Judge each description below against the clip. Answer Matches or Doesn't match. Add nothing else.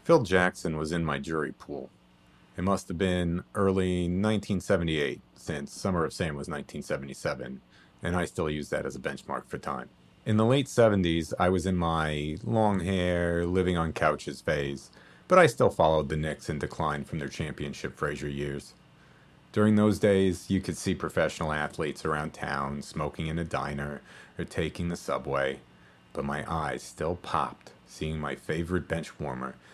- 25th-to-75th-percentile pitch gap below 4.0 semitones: Doesn't match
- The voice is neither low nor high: Doesn't match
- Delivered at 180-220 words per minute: Doesn't match